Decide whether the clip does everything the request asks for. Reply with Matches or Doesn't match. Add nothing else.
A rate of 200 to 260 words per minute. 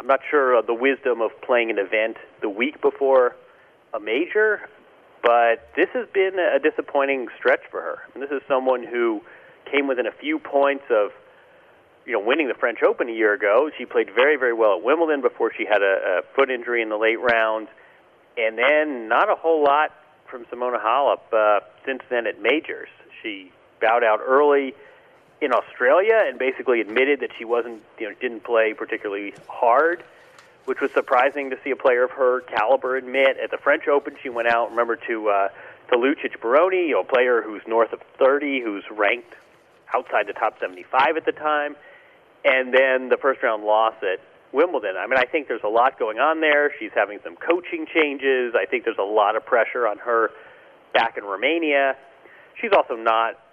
Doesn't match